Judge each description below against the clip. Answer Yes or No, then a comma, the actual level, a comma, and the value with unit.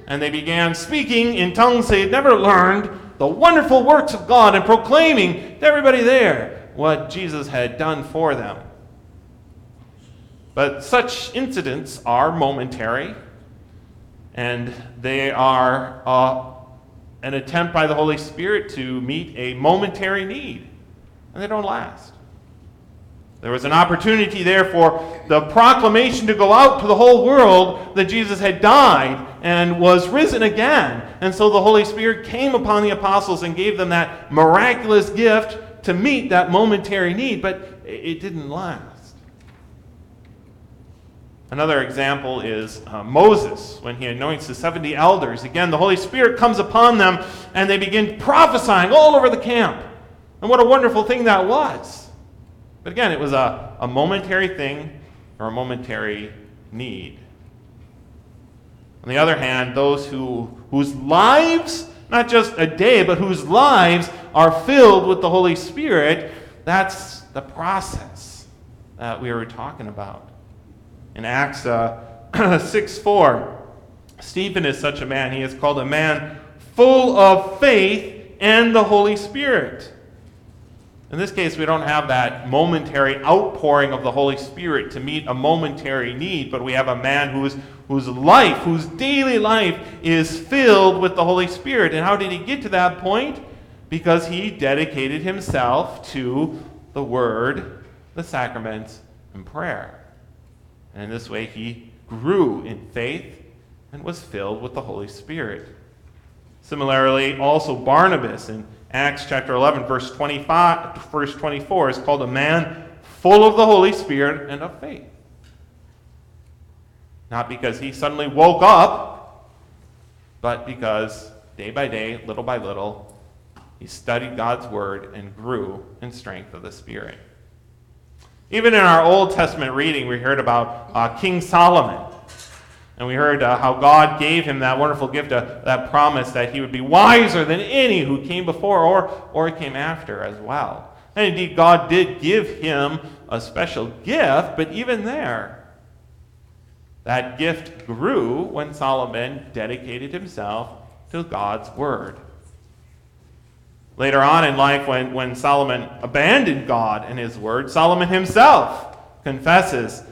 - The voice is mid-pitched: Yes, medium, 150 Hz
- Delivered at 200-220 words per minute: No, average, 145 wpm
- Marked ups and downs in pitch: Yes, wide, 7.5 semitones